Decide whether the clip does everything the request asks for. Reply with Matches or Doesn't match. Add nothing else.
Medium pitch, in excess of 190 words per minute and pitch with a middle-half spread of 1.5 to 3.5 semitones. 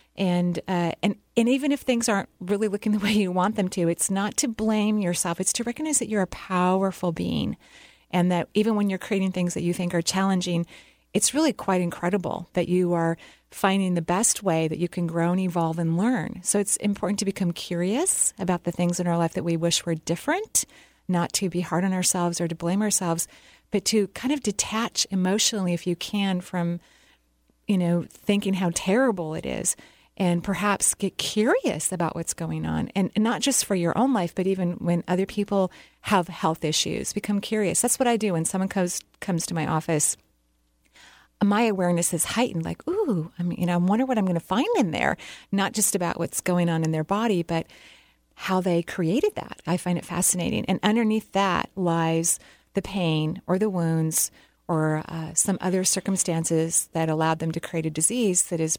Matches